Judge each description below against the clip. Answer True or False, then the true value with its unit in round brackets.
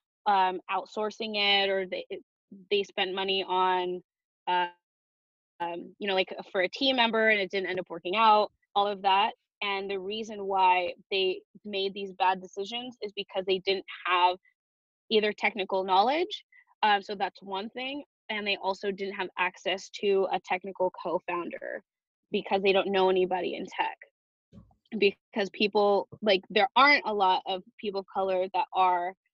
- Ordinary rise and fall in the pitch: False (2.2 semitones)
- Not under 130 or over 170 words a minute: True (165 wpm)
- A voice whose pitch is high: True (195 Hz)